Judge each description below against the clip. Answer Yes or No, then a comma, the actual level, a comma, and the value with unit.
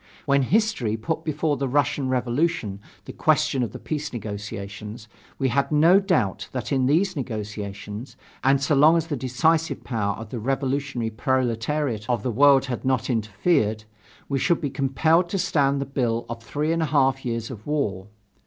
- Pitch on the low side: Yes, low, 130 Hz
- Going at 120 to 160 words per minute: No, average, 175 wpm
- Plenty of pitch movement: No, average, 4.6 semitones